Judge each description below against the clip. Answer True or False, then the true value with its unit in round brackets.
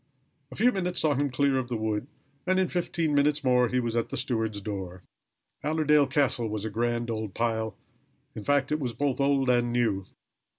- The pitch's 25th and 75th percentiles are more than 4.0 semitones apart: True (4.4 semitones)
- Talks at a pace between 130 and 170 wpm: False (200 wpm)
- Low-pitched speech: True (125 Hz)